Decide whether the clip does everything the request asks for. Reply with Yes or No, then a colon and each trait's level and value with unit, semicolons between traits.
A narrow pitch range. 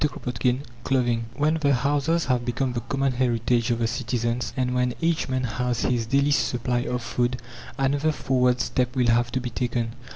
Yes: narrow, 2.0 semitones